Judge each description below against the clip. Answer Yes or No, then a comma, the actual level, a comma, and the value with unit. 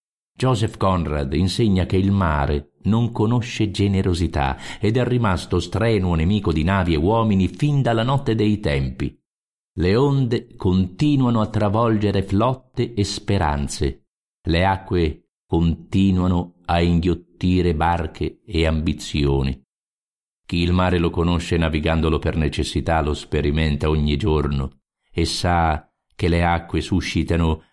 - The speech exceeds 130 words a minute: No, average, 125 wpm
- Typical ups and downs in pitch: Yes, average, 4.7 semitones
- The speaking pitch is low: Yes, very low, 90 Hz